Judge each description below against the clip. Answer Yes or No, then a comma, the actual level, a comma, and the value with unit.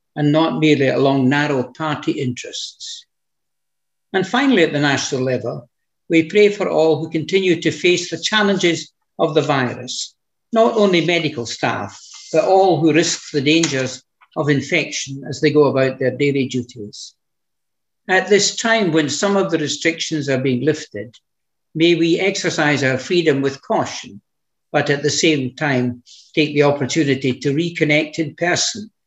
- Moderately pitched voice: Yes, medium, 155 Hz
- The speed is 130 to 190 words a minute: Yes, average, 155 wpm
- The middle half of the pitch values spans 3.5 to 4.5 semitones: Yes, average, 3.8 semitones